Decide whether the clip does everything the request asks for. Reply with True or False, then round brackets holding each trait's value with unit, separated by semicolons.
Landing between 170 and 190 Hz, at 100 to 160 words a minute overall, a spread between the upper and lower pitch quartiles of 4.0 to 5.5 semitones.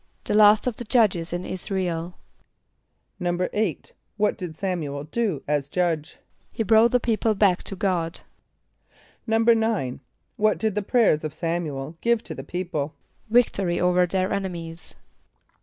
True (185 Hz; 150 wpm; 4.6 semitones)